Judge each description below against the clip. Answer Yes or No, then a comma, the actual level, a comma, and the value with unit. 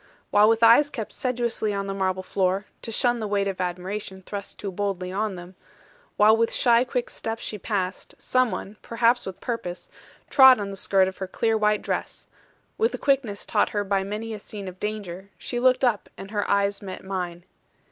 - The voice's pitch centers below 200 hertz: No, high, 205 Hz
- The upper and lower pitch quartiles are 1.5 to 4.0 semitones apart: Yes, average, 3.1 semitones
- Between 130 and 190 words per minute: No, average, 200 wpm